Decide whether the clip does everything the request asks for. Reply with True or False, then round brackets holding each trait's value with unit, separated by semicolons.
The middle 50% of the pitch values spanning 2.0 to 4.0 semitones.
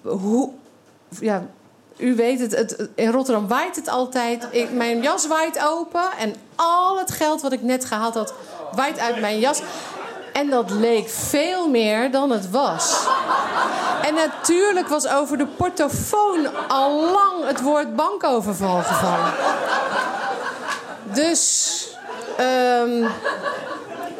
False (4.9 semitones)